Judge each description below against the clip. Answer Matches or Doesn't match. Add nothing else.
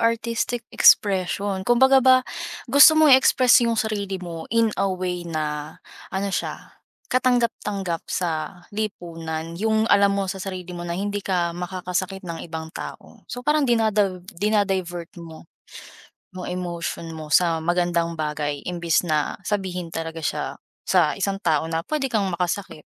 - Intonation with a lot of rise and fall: Doesn't match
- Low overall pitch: Doesn't match